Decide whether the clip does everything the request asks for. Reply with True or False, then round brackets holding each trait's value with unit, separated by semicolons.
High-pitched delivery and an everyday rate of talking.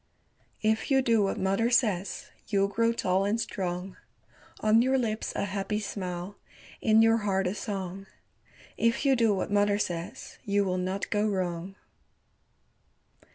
True (205 Hz; 150 wpm)